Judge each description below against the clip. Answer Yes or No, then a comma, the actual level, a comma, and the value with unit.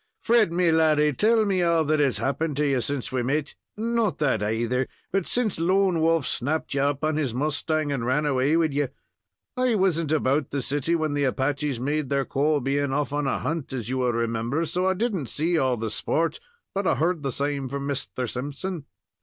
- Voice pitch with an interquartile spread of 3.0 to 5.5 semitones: Yes, average, 3.8 semitones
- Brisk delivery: Yes, fast, 210 wpm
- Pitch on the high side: No, medium, 145 Hz